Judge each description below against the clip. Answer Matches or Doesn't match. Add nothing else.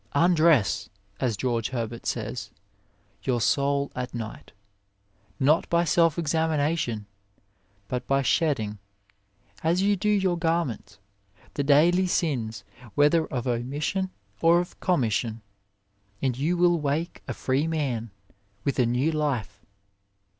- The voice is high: Doesn't match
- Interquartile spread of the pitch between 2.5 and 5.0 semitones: Doesn't match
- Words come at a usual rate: Doesn't match